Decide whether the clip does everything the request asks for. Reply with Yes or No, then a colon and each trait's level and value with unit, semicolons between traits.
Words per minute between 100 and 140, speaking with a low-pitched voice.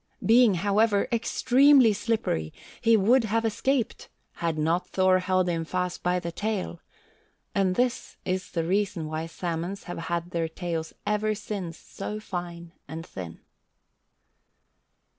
No: slow, 135 wpm; medium, 185 Hz